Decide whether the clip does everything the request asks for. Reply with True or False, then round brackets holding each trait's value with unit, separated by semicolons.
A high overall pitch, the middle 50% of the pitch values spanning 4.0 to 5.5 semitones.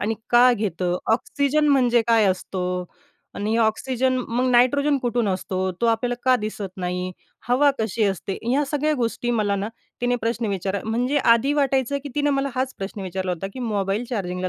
True (230 Hz; 4.6 semitones)